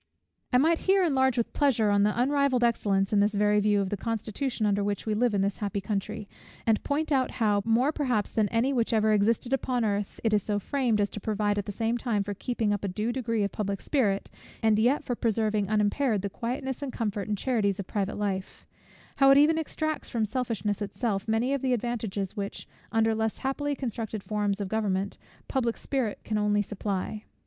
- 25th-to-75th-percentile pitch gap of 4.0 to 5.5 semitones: No, average, 3.4 semitones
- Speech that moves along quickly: Yes, fast, 210 wpm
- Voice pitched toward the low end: No, high, 220 Hz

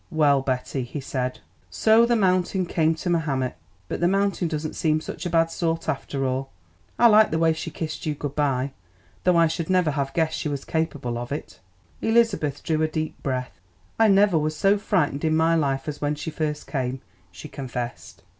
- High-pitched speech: No, medium, 155 Hz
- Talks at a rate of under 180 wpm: No, average, 200 wpm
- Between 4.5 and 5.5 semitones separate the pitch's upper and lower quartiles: No, average, 3.7 semitones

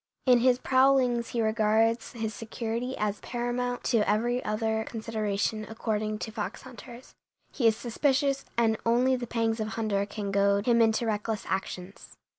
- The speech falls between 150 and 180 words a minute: Yes, average, 155 wpm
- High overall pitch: Yes, high, 225 Hz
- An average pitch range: No, narrow, 2.2 semitones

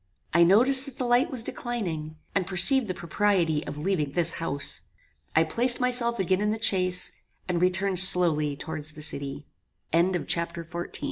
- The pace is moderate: Yes, average, 165 wpm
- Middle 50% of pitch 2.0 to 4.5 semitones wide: No, wide, 5.4 semitones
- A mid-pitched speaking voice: Yes, medium, 180 Hz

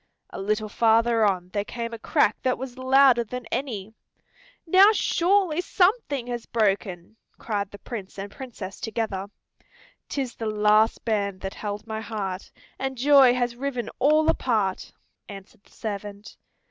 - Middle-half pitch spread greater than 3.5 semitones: Yes, average, 4.1 semitones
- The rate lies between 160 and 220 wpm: No, average, 145 wpm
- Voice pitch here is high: Yes, high, 225 Hz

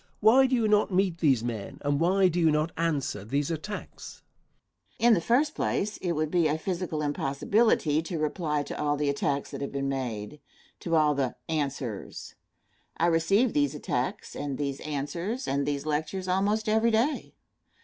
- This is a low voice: No, medium, 155 Hz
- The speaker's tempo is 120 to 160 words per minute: No, average, 180 wpm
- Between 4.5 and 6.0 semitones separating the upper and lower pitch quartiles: Yes, average, 5.2 semitones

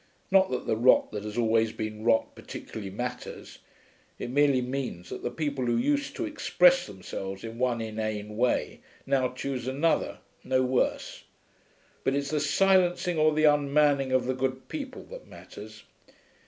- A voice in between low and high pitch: No, low, 130 Hz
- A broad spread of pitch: No, average, 4.6 semitones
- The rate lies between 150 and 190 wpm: Yes, average, 160 wpm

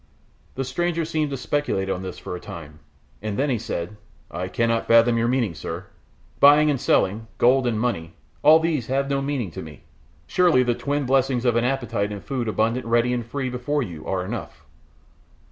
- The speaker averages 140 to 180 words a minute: No, average, 195 wpm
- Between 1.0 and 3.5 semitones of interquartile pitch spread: No, average, 4.5 semitones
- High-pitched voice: No, low, 120 Hz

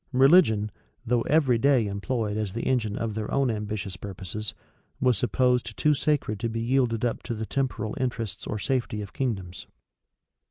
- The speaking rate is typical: Yes, average, 170 wpm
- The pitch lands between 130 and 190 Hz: No, low, 115 Hz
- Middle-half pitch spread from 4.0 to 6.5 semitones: No, average, 3.4 semitones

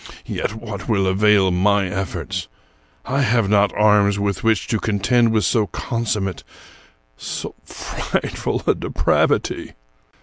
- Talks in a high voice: No, low, 105 Hz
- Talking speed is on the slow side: Yes, slow, 125 wpm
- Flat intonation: Yes, narrow, 2.3 semitones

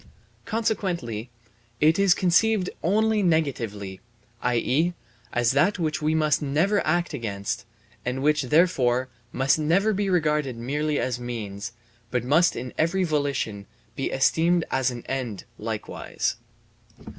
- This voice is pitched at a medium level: Yes, medium, 150 Hz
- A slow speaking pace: Yes, slow, 125 wpm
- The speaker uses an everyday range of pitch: No, wide, 6.0 semitones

